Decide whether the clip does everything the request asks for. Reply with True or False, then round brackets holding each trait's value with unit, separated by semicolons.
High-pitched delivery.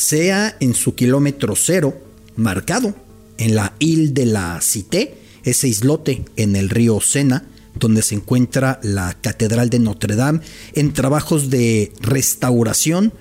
False (120 Hz)